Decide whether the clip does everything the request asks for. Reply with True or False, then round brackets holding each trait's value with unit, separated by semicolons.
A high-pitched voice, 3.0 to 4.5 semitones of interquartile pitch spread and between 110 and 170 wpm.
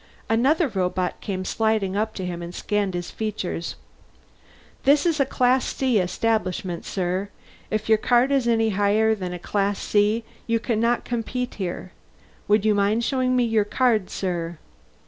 True (215 Hz; 4.0 semitones; 155 wpm)